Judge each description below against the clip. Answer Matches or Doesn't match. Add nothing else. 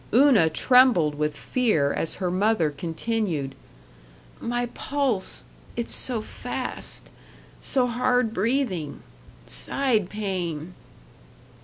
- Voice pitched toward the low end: Doesn't match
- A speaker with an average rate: Doesn't match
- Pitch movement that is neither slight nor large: Doesn't match